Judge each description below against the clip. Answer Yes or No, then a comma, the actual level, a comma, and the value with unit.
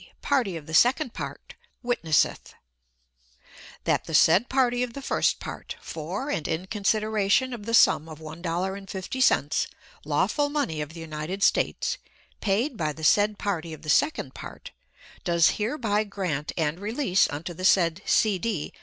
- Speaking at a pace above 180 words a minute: No, average, 155 wpm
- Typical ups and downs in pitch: No, wide, 6.1 semitones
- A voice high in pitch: Yes, high, 195 Hz